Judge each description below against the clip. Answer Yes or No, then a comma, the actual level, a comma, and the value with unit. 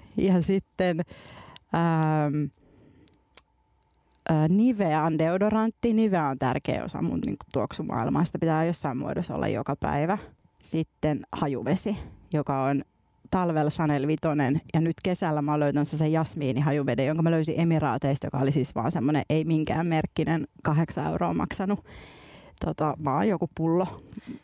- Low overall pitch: No, medium, 160 Hz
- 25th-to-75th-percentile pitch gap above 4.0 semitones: No, average, 3.0 semitones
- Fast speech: No, average, 140 wpm